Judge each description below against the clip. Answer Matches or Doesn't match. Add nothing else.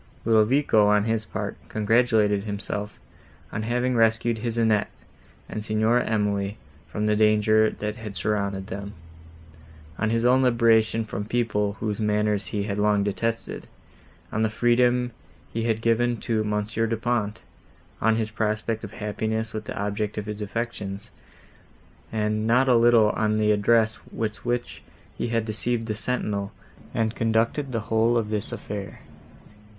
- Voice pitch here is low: Matches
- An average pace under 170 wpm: Matches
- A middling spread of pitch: Doesn't match